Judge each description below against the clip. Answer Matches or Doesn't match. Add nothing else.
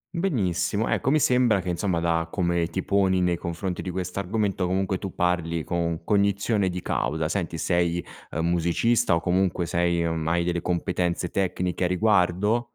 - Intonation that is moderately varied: Doesn't match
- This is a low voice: Matches